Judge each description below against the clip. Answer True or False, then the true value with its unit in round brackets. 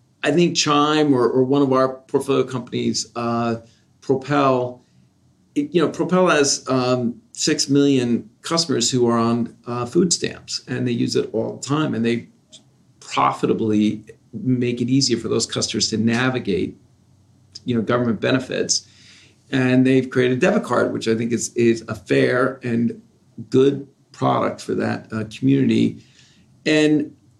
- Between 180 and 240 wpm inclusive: False (150 wpm)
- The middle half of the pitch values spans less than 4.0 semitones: True (3.1 semitones)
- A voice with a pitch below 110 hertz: False (125 Hz)